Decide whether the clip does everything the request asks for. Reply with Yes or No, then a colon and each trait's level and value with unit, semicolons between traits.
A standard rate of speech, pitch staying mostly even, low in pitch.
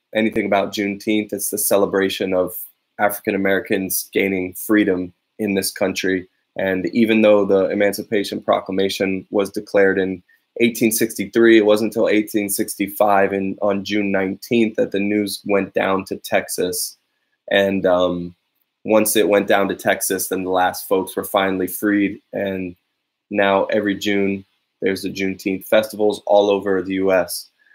Yes: average, 145 wpm; narrow, 1.7 semitones; low, 100 Hz